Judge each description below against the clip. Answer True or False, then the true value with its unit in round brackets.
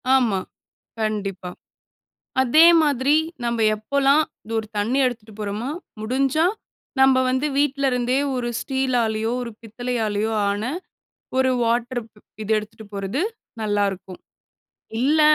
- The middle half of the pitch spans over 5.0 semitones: False (3.7 semitones)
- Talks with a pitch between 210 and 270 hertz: True (235 Hz)